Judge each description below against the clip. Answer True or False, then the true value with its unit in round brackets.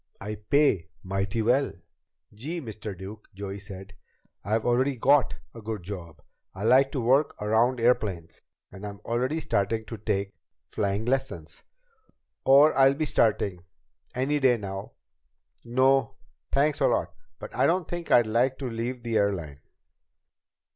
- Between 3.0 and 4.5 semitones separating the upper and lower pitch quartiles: False (4.9 semitones)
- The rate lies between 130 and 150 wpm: True (145 wpm)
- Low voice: True (115 Hz)